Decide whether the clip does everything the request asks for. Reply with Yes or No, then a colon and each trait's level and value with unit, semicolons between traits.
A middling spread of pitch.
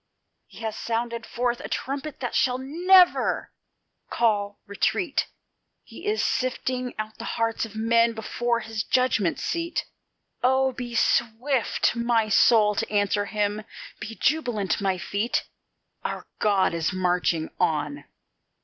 Yes: average, 3.6 semitones